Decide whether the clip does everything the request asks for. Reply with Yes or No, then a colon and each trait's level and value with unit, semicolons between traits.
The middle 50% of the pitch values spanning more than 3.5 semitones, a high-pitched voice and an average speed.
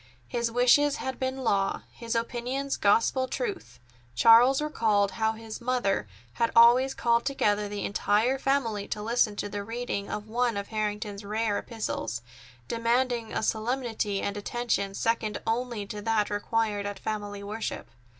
No: average, 2.9 semitones; high, 225 Hz; average, 150 wpm